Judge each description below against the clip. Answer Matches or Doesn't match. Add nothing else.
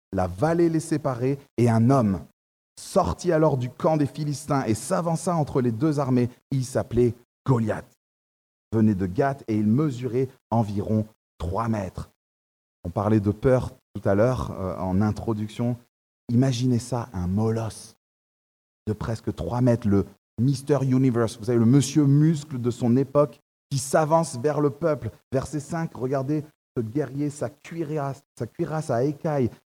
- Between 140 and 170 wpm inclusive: Matches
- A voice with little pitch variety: Doesn't match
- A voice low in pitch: Matches